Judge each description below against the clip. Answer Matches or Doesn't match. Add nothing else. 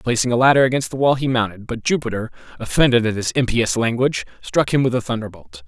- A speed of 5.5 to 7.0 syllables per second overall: Matches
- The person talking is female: Doesn't match